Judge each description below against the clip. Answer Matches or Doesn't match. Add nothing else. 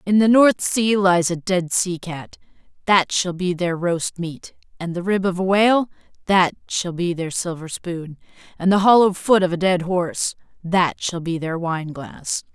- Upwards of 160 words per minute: Matches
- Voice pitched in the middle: Matches